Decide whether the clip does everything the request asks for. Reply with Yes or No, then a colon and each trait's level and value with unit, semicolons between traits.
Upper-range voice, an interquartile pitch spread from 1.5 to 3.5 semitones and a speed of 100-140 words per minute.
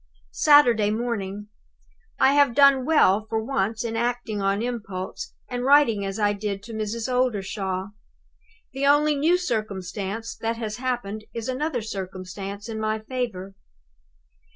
No: high, 220 Hz; average, 3.9 semitones; slow, 135 wpm